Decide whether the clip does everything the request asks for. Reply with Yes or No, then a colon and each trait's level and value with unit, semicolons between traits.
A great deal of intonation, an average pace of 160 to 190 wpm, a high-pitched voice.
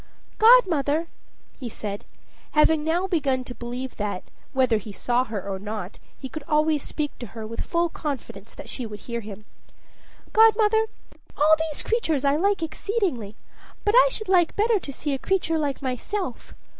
Yes: wide, 6.7 semitones; average, 170 wpm; very high, 290 Hz